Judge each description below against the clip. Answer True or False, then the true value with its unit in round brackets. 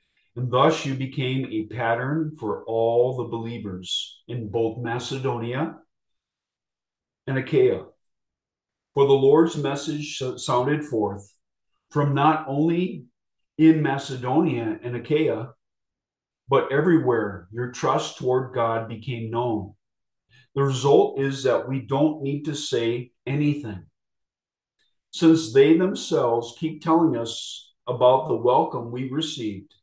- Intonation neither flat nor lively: True (4.2 semitones)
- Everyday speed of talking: False (115 wpm)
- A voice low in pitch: True (130 Hz)